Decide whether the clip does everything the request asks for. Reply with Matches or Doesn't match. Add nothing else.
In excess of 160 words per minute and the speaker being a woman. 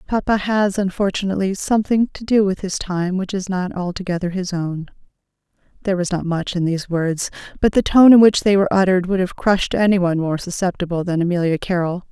Matches